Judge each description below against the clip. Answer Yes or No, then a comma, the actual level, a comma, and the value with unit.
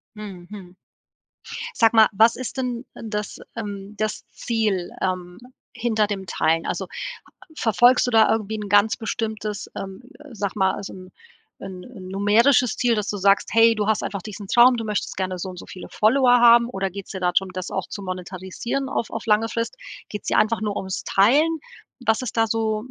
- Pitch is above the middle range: Yes, high, 210 Hz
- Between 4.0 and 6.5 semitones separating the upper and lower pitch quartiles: No, average, 3.0 semitones